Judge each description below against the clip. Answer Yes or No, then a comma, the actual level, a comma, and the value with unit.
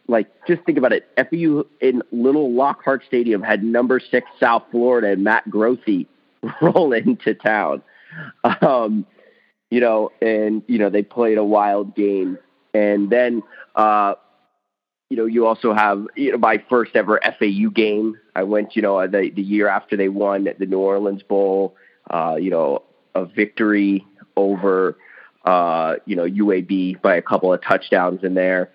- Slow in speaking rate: No, average, 165 wpm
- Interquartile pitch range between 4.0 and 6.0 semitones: No, average, 3.3 semitones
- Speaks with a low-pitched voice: Yes, low, 105 Hz